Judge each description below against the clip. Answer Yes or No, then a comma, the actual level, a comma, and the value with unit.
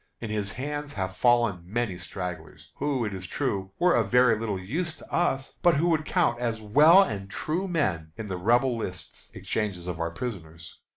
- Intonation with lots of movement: Yes, wide, 7.1 semitones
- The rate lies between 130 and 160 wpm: No, average, 190 wpm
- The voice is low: Yes, low, 115 Hz